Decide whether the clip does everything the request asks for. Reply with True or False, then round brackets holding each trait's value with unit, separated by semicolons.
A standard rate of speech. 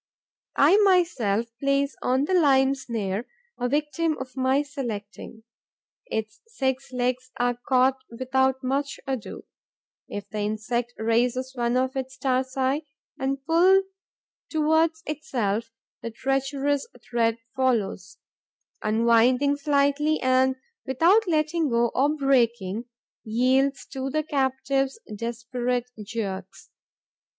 False (110 wpm)